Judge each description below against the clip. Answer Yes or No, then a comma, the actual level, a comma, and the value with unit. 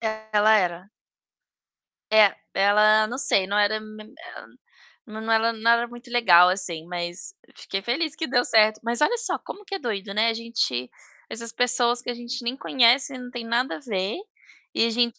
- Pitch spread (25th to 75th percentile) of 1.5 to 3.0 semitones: Yes, average, 2.7 semitones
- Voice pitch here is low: No, high, 230 Hz